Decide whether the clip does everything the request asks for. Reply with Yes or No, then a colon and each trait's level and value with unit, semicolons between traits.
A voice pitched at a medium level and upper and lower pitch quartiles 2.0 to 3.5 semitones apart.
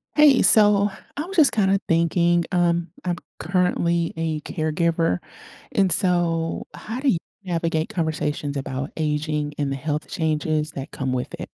Yes: medium, 165 Hz; average, 2.9 semitones